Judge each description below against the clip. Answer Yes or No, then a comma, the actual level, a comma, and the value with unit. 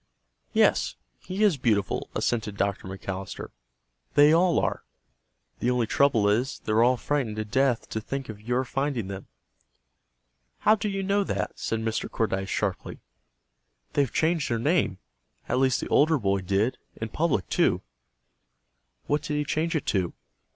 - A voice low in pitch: Yes, low, 120 Hz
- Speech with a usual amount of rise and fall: No, wide, 6.1 semitones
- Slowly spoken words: No, average, 155 wpm